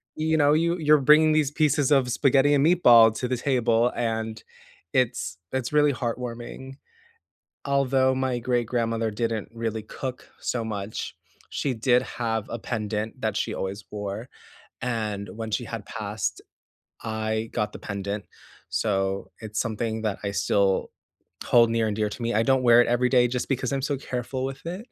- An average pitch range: Yes, average, 3.2 semitones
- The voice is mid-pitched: No, low, 120 Hz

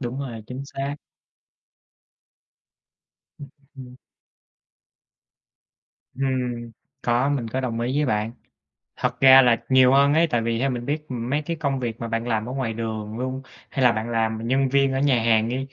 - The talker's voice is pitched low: Yes, low, 125 Hz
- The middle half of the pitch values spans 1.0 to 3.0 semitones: Yes, average, 2.7 semitones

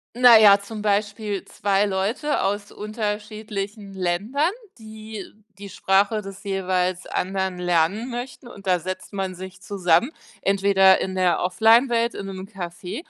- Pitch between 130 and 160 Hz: No, high, 200 Hz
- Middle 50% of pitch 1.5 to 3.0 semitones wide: Yes, narrow, 2.4 semitones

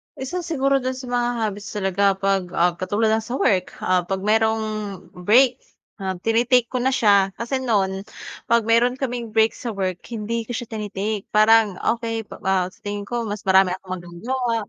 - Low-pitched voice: No, high, 220 Hz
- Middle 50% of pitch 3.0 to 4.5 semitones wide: Yes, average, 3.7 semitones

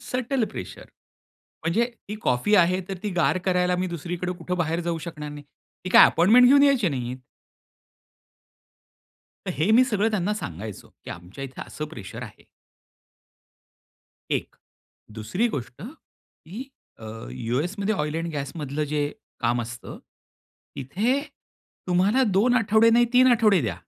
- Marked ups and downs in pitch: Yes, wide, 7.0 semitones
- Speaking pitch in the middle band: Yes, medium, 180 Hz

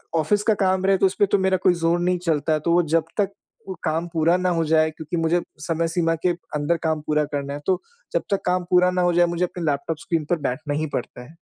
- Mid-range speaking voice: Yes, medium, 170 Hz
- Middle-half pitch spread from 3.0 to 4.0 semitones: No, narrow, 2.5 semitones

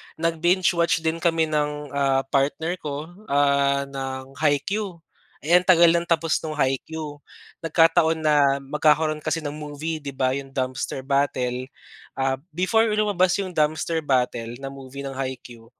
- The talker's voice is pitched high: No, medium, 150 Hz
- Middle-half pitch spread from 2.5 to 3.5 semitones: Yes, average, 3.2 semitones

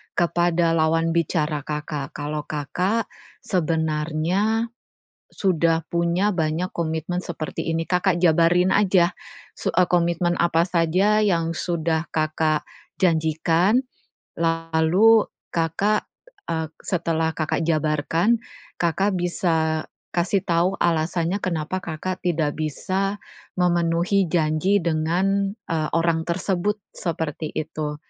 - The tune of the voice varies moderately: No, narrow, 2.3 semitones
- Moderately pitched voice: Yes, medium, 170 Hz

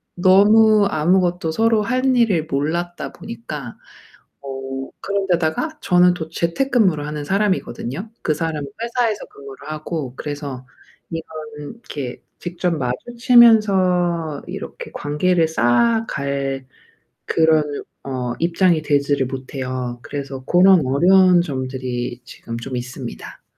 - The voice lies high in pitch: No, medium, 160 Hz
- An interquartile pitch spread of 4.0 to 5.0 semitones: No, wide, 5.5 semitones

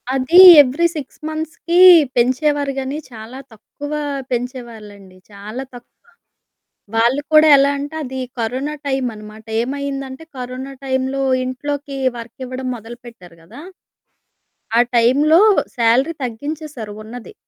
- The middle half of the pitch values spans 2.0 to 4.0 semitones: Yes, average, 3.4 semitones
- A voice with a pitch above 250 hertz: Yes, very high, 260 Hz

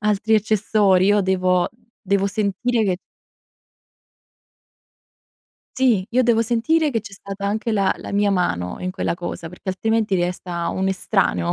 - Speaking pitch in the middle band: No, high, 200 Hz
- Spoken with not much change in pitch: No, average, 3.1 semitones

